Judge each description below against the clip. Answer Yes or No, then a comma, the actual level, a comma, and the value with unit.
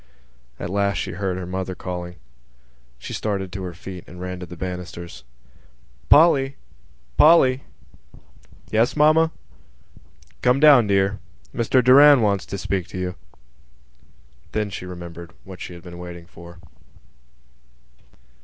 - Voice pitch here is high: No, very low, 95 Hz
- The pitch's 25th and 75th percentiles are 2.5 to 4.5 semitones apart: No, average, 4.9 semitones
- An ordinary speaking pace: No, slow, 130 wpm